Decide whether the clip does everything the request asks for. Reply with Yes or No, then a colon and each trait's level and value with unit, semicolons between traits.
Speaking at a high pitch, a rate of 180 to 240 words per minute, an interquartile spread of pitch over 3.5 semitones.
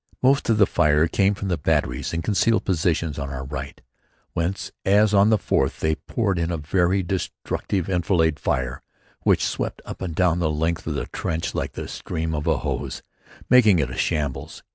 No: very low, 85 Hz; average, 190 wpm; average, 4.0 semitones